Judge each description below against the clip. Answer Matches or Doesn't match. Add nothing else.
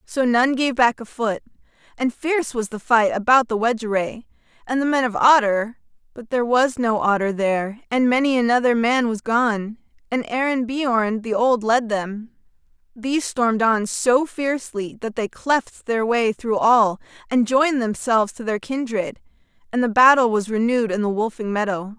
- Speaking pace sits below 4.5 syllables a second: Doesn't match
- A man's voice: Doesn't match